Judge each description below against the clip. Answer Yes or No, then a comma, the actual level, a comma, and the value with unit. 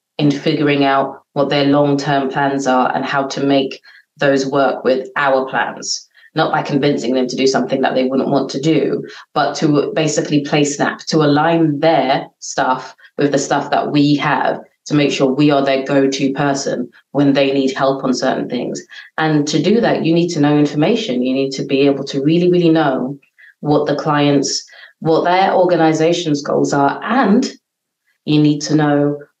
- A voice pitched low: No, medium, 145 Hz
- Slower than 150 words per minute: No, average, 190 wpm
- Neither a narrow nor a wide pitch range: No, narrow, 1.8 semitones